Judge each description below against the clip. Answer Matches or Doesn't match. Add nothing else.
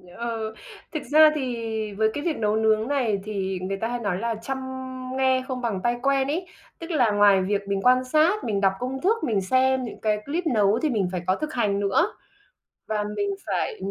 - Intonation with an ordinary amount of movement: Matches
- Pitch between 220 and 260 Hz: Matches